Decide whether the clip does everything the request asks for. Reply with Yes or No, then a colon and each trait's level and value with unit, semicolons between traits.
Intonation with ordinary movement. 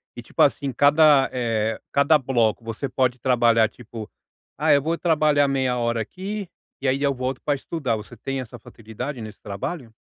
Yes: average, 3.8 semitones